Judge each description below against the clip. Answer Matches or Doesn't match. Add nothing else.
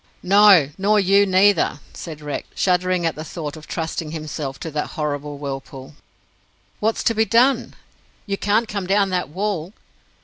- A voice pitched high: Doesn't match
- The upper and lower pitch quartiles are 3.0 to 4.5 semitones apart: Doesn't match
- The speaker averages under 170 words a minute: Matches